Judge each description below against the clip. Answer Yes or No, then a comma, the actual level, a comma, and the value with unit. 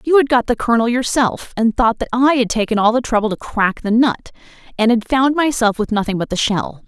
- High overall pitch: Yes, high, 235 Hz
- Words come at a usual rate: No, fast, 245 wpm